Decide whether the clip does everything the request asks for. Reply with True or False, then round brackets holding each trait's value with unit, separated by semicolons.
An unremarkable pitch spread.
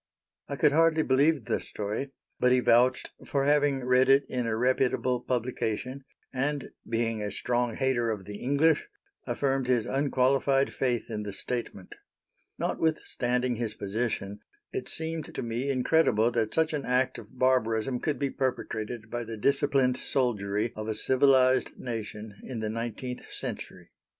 True (3.2 semitones)